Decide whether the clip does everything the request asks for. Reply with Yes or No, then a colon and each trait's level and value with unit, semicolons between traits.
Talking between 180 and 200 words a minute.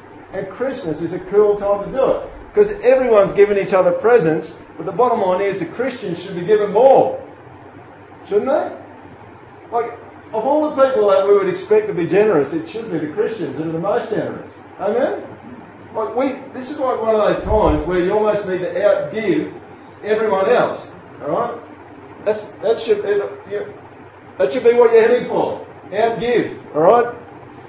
Yes: average, 185 wpm